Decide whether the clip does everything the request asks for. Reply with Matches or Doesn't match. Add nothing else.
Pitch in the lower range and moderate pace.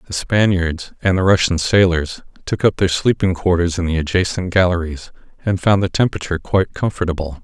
Matches